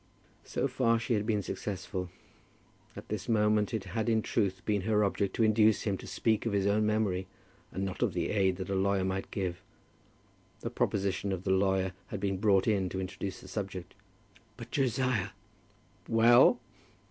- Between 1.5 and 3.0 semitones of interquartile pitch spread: Yes, narrow, 2.5 semitones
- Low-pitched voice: Yes, low, 100 Hz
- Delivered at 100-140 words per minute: No, average, 180 wpm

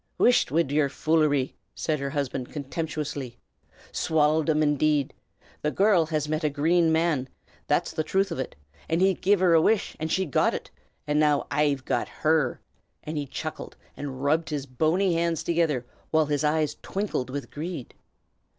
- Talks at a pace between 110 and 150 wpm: No, average, 170 wpm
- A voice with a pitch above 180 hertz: No, medium, 155 Hz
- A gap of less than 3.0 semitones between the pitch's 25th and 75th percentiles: Yes, narrow, 2.5 semitones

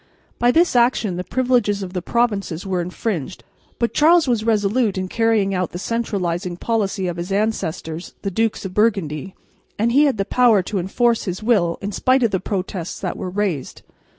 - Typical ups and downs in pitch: Yes, average, 4.2 semitones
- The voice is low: No, high, 200 Hz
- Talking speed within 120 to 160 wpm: No, average, 185 wpm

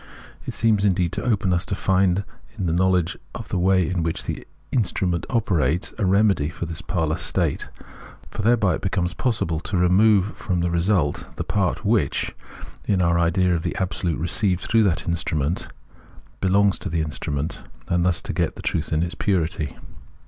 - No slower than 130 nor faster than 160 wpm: No, average, 185 wpm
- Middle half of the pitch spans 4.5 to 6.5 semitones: No, average, 2.7 semitones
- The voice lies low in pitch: Yes, very low, 90 Hz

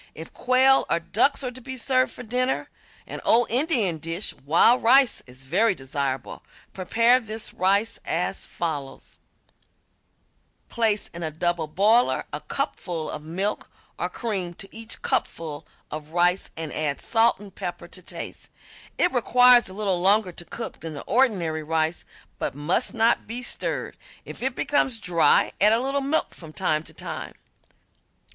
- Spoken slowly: No, average, 160 wpm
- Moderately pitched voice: No, high, 200 Hz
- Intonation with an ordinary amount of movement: No, wide, 6.8 semitones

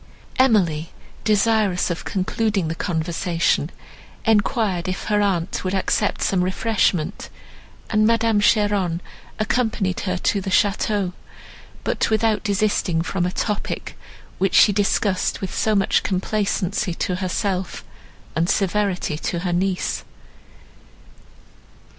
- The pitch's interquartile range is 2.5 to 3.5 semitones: Yes, average, 2.8 semitones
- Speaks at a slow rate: Yes, slow, 115 wpm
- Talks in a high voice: Yes, high, 195 Hz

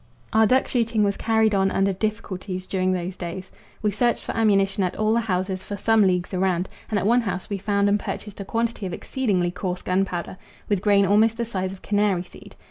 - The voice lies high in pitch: Yes, high, 200 Hz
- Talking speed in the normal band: No, fast, 210 wpm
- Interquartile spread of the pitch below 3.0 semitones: Yes, narrow, 2.6 semitones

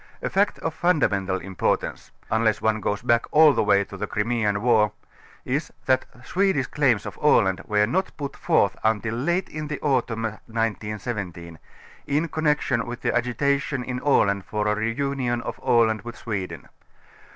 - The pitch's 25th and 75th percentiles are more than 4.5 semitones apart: Yes, average, 4.9 semitones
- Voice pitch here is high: No, low, 115 Hz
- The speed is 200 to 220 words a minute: No, average, 170 wpm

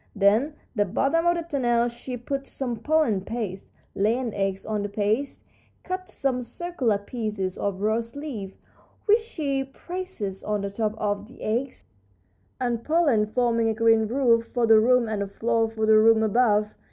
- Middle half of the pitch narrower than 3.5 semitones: No, average, 4.2 semitones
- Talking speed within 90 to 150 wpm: No, average, 175 wpm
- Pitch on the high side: Yes, high, 230 Hz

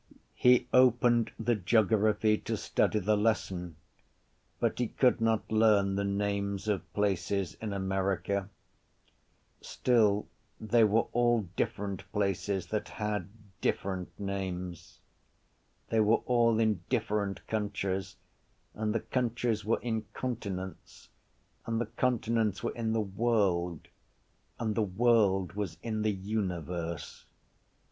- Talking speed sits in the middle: No, slow, 120 wpm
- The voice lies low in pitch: Yes, low, 105 Hz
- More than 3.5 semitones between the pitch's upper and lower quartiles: No, average, 2.7 semitones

